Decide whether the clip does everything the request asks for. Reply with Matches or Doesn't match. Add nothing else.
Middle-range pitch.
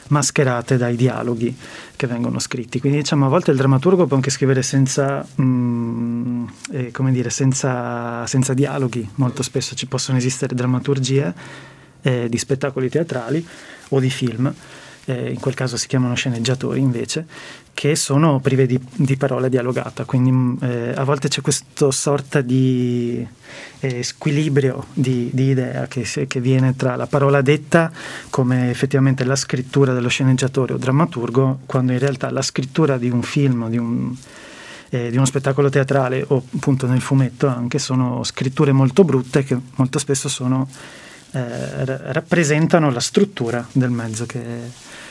Doesn't match